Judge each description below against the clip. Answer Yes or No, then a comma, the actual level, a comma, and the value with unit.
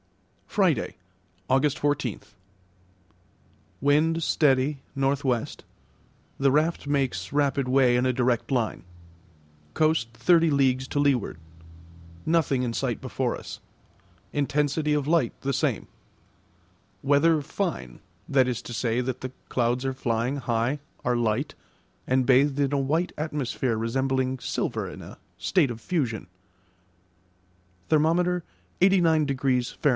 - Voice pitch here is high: No, low, 135 Hz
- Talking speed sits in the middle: No, slow, 120 wpm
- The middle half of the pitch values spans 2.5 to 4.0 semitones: Yes, average, 3.0 semitones